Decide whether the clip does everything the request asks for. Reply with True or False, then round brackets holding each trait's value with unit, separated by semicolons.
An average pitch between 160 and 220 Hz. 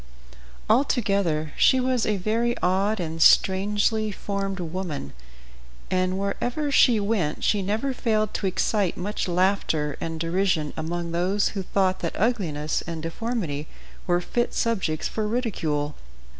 True (190 Hz)